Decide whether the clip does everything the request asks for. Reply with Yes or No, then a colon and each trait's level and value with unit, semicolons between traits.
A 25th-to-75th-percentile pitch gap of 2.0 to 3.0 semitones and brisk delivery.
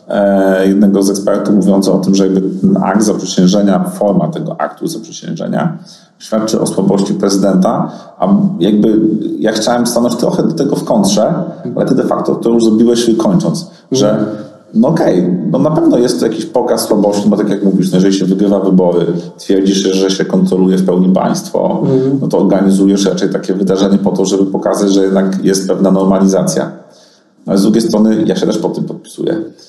Yes: narrow, 2.5 semitones; fast, 185 wpm